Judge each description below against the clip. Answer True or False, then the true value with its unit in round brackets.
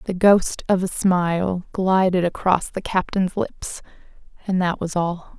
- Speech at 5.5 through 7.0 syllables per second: False (4.1 syllables/s)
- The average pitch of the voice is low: False (185 Hz)